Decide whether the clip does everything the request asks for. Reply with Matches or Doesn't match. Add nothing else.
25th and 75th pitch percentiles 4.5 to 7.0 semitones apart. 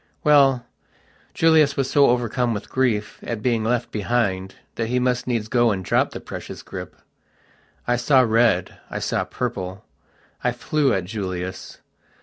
Doesn't match